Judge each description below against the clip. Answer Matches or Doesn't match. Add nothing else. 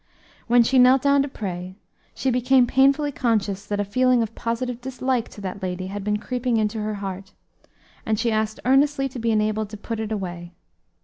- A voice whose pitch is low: Doesn't match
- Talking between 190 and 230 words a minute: Matches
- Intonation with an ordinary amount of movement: Matches